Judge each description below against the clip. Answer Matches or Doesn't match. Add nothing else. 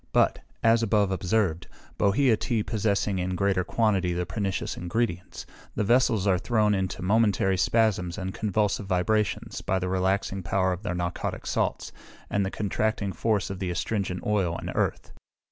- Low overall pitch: Matches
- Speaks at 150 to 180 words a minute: Matches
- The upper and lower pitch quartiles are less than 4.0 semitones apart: Matches